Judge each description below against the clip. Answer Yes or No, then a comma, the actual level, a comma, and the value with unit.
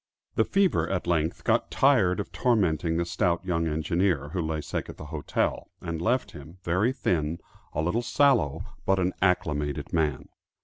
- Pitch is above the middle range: No, very low, 85 Hz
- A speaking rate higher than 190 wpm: No, average, 170 wpm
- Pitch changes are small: No, average, 3.6 semitones